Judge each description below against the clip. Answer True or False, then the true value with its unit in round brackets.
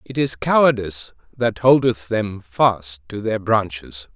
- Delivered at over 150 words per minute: False (145 wpm)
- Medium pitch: False (105 Hz)